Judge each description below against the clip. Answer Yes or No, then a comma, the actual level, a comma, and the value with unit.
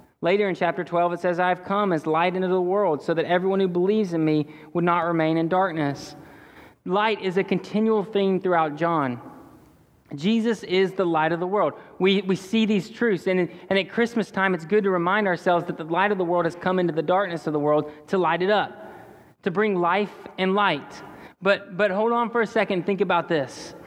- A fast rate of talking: Yes, fast, 220 wpm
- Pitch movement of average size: Yes, average, 3.0 semitones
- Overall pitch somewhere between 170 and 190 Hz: Yes, medium, 185 Hz